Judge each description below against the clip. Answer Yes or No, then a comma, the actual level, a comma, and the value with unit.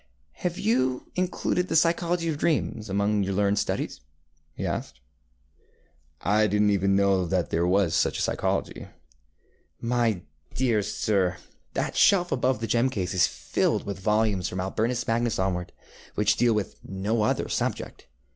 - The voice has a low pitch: Yes, low, 105 Hz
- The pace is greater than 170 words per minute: No, average, 155 wpm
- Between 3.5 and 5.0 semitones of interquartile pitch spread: Yes, average, 4.4 semitones